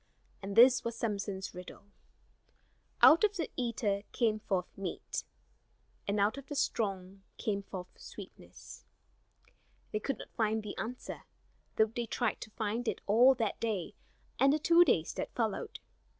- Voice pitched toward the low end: No, high, 220 Hz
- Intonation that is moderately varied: Yes, average, 3.6 semitones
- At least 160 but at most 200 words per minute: No, average, 150 wpm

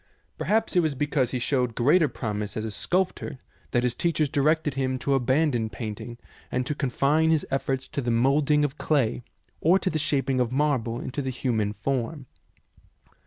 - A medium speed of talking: Yes, average, 185 wpm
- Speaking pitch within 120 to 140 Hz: Yes, low, 135 Hz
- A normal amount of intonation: Yes, average, 3.7 semitones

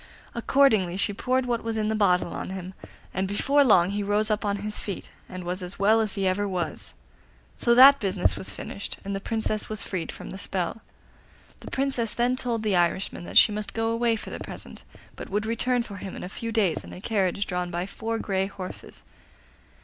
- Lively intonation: No, average, 3.2 semitones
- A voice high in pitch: Yes, high, 205 Hz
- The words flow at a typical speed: No, fast, 215 wpm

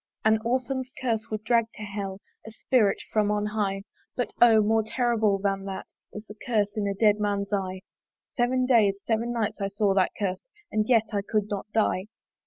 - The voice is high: Yes, high, 210 Hz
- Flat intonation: Yes, narrow, 2.3 semitones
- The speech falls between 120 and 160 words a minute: No, average, 195 wpm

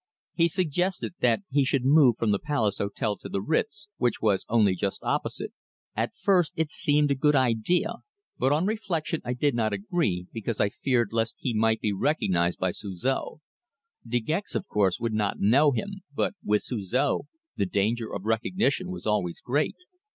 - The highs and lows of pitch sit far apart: Yes, wide, 6.5 semitones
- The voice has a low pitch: Yes, low, 120 Hz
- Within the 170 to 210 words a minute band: Yes, average, 180 wpm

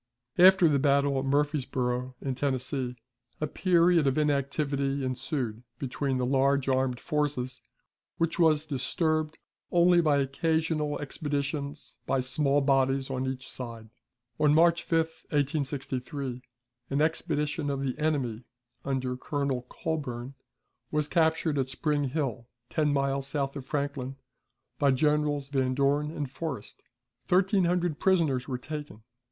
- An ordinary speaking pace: No, slow, 130 wpm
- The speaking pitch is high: No, medium, 140 Hz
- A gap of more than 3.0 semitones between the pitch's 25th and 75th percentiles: No, narrow, 2.5 semitones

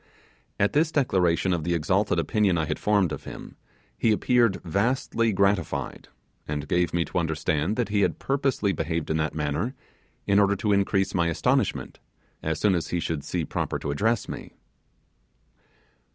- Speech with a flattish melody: No, average, 4.4 semitones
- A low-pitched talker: Yes, very low, 95 Hz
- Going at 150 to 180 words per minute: Yes, average, 165 wpm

